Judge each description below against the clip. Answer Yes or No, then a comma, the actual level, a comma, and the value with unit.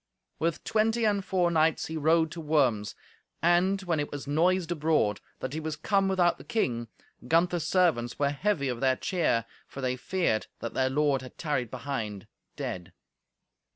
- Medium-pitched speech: Yes, medium, 155 Hz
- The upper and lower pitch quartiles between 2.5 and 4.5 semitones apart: No, average, 5.1 semitones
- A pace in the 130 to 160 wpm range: No, average, 170 wpm